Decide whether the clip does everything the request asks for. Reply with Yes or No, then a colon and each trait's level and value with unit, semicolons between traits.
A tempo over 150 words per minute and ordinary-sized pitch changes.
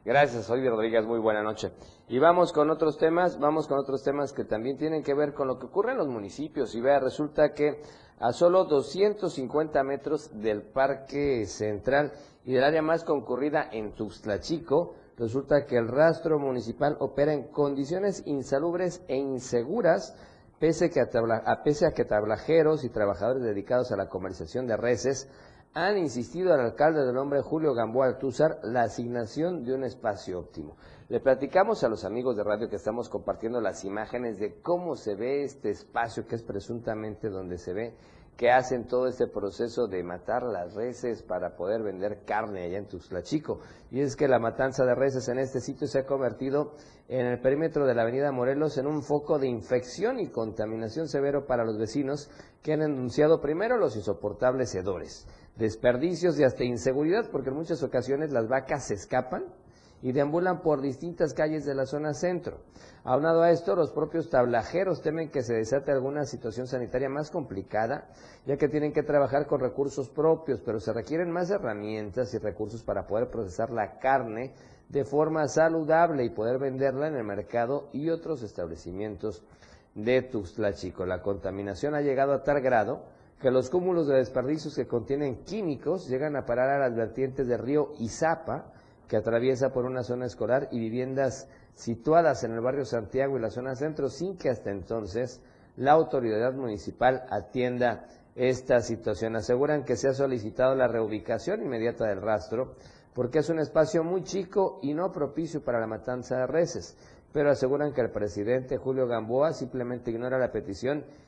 Yes: average, 175 wpm; average, 4.3 semitones